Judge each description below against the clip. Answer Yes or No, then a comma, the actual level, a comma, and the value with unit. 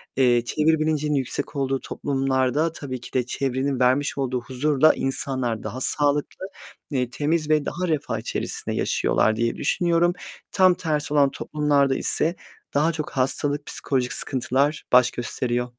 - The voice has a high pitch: No, medium, 140 Hz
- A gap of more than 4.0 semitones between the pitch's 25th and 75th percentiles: No, average, 3.0 semitones